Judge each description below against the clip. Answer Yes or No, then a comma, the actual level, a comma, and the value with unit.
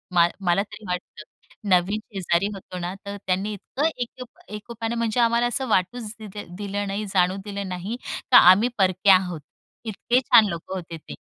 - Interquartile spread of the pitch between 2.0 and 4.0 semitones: Yes, average, 3.6 semitones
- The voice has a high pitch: Yes, high, 200 Hz